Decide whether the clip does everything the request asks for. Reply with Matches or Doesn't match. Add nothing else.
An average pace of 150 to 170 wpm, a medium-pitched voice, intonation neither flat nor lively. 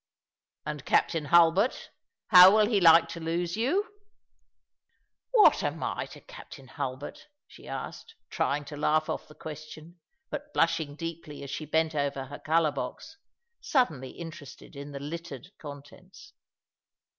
Matches